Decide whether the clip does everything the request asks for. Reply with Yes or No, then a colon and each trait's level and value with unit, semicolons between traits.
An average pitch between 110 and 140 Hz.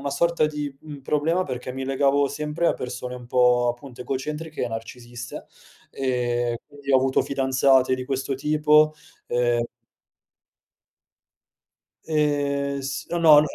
Yes: low, 135 Hz